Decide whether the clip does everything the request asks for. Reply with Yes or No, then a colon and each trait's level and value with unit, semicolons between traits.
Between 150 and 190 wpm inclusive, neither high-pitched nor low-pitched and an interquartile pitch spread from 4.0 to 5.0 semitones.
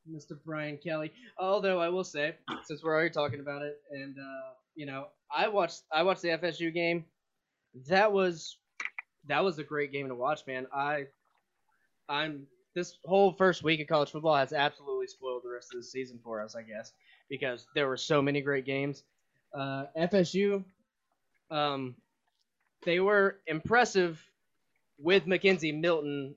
Yes: average, 160 wpm; medium, 155 Hz; average, 4.5 semitones